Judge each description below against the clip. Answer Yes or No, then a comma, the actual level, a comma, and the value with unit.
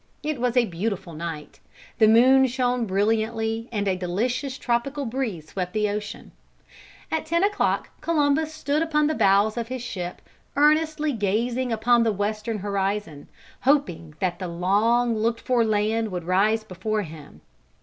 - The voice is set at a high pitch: Yes, high, 225 Hz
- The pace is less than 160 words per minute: Yes, average, 150 wpm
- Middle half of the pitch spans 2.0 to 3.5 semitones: No, average, 4.6 semitones